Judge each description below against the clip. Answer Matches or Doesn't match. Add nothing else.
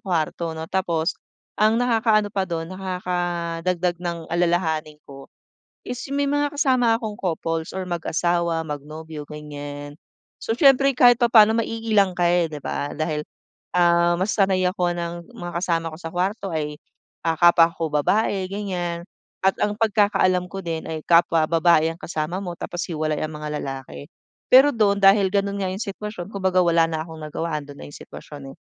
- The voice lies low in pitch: Doesn't match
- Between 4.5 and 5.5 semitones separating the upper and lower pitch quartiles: Doesn't match